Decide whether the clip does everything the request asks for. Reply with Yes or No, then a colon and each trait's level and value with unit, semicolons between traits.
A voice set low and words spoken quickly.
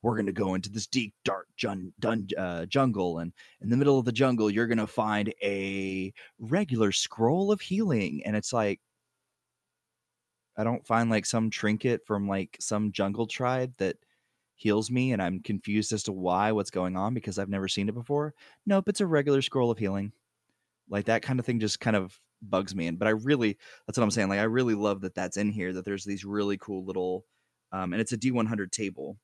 Yes: low, 110 Hz; fast, 215 wpm